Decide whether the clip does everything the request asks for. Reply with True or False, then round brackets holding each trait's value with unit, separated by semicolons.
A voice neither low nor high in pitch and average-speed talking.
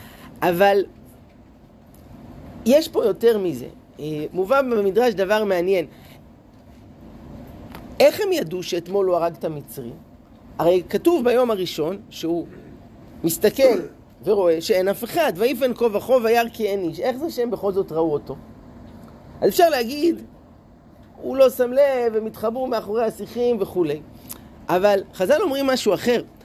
False (215 Hz; 135 wpm)